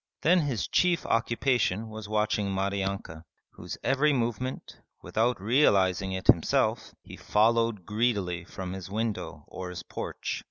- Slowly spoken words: Yes, slow, 130 wpm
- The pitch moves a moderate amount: Yes, average, 3.8 semitones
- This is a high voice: No, low, 105 Hz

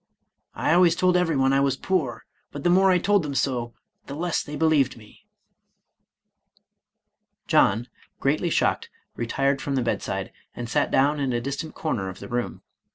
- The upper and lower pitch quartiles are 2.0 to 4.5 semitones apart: No, average, 4.9 semitones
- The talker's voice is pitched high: No, medium, 140 Hz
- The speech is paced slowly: No, average, 170 wpm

